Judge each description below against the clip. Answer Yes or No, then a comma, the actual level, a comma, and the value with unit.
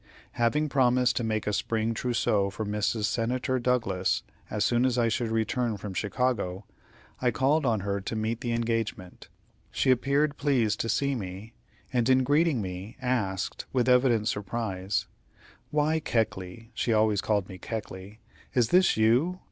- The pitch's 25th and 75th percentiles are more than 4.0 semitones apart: No, average, 3.4 semitones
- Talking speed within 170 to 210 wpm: No, average, 155 wpm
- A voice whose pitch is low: Yes, low, 115 Hz